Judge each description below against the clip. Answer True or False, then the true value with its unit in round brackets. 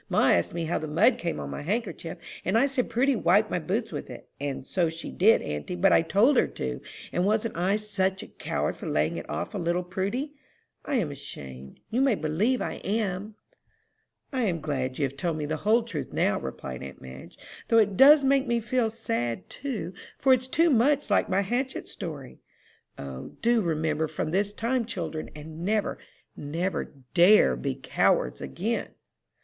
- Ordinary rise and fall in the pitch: False (6.7 semitones)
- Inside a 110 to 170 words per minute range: False (190 wpm)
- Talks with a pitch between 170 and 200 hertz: True (190 Hz)